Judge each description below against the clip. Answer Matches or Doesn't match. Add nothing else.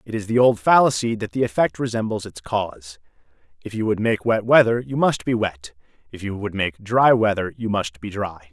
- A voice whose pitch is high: Doesn't match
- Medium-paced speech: Doesn't match